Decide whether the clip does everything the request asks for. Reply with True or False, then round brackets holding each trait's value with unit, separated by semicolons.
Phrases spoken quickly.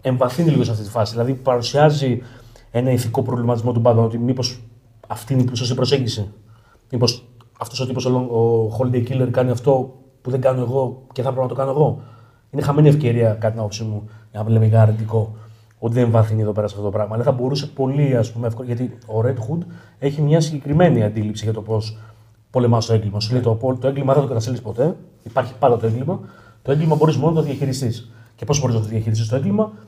True (220 wpm)